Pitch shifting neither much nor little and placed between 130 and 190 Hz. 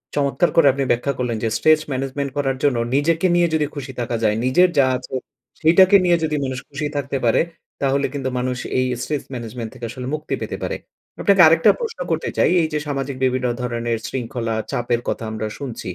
Yes: average, 3.7 semitones; low, 135 Hz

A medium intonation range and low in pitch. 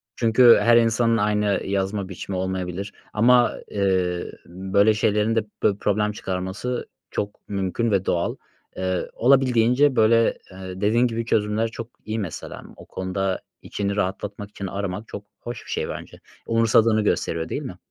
Yes: average, 3.2 semitones; low, 105 Hz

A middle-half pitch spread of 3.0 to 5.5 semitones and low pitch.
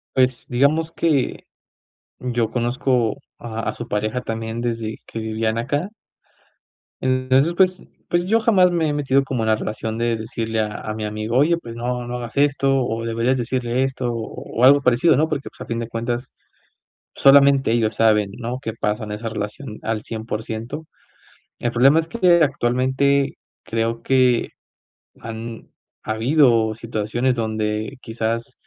Yes: average, 3.3 semitones; low, 120 Hz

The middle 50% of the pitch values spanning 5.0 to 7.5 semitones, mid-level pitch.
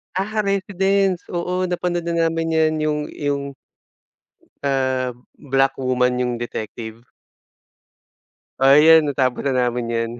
Yes: average, 5.3 semitones; medium, 145 Hz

